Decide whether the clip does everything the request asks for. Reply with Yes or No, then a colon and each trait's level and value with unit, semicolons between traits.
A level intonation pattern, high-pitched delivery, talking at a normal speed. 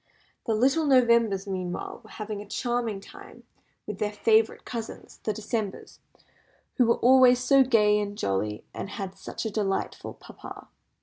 No: average, 3.1 semitones; high, 215 Hz; average, 150 wpm